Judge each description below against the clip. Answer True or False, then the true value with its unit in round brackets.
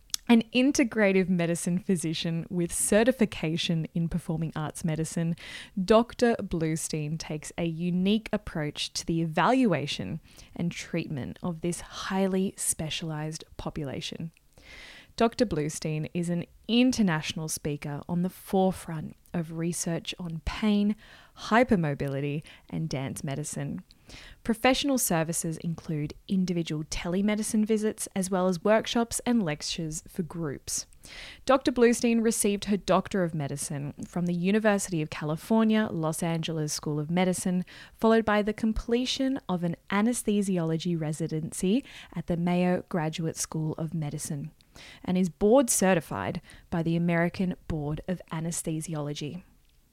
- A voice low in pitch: False (175 Hz)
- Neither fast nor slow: False (120 wpm)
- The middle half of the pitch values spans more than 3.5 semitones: True (4.6 semitones)